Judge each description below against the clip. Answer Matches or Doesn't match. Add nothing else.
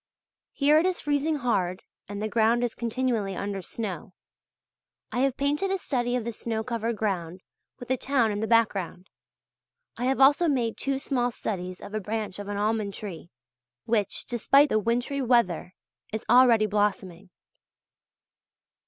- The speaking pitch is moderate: Doesn't match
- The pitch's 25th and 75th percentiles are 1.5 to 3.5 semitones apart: Doesn't match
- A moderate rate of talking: Matches